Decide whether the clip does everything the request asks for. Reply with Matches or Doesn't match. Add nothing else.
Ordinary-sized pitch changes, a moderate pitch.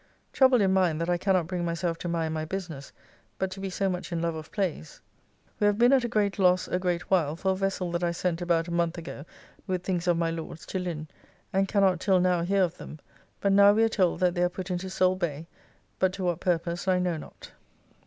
Doesn't match